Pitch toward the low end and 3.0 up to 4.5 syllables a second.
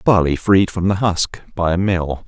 Yes: very low, 90 Hz; 4.4 syllables/s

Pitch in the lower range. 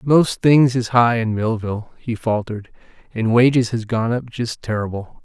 Yes: low, 115 Hz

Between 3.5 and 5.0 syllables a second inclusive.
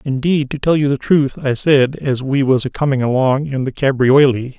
Yes: 4.9 syllables/s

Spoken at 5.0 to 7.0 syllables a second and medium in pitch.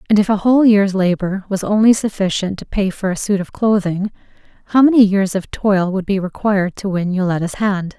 No: 5.5 syllables/s; high, 195 Hz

